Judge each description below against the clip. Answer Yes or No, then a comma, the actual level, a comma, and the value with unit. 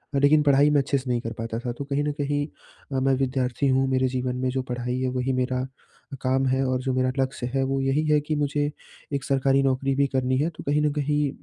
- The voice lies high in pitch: No, low, 135 Hz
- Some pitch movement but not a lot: No, narrow, 1.8 semitones